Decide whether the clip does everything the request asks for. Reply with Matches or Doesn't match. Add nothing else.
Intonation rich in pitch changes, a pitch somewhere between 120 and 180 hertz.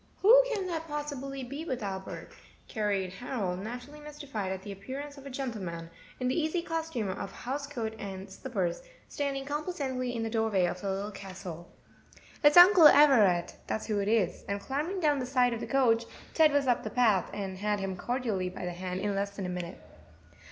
Doesn't match